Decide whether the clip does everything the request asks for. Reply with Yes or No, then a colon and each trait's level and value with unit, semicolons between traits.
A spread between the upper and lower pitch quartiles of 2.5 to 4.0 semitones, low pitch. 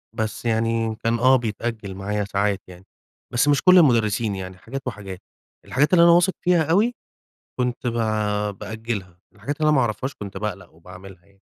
No: average, 5.0 semitones; low, 110 Hz